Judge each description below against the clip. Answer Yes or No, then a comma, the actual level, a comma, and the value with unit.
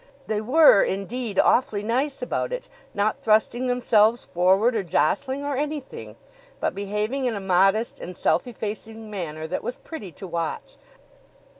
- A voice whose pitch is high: Yes, high, 215 Hz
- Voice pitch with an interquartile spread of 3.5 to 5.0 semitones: Yes, average, 4.3 semitones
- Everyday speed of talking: Yes, average, 150 wpm